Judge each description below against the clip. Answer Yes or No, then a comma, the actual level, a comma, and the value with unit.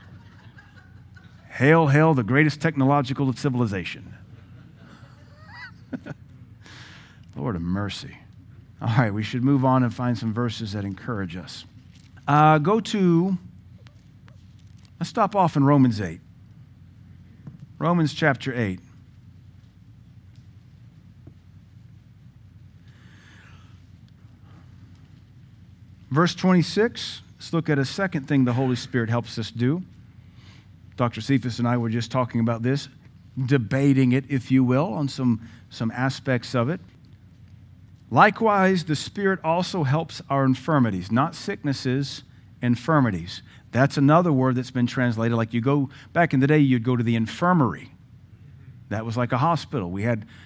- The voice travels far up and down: No, average, 4.3 semitones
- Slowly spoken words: Yes, slow, 120 wpm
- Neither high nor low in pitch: No, low, 120 Hz